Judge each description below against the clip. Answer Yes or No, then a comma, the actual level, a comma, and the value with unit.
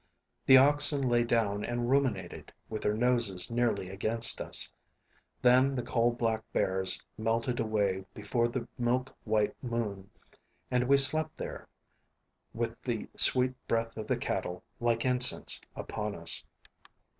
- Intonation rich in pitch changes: No, average, 2.9 semitones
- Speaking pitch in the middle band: No, low, 115 Hz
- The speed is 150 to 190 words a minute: No, slow, 135 wpm